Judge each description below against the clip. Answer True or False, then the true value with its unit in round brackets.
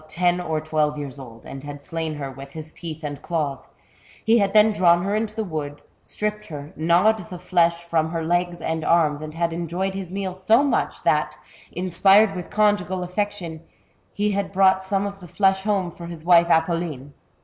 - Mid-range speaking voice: True (175 Hz)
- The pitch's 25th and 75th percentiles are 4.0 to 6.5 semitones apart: False (3.6 semitones)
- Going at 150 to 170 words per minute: False (195 wpm)